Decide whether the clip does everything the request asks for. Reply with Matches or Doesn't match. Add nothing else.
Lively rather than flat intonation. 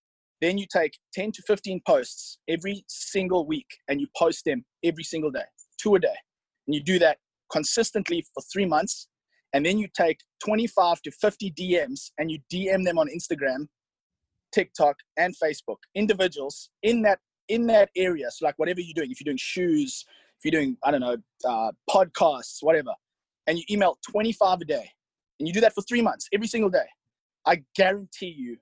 Doesn't match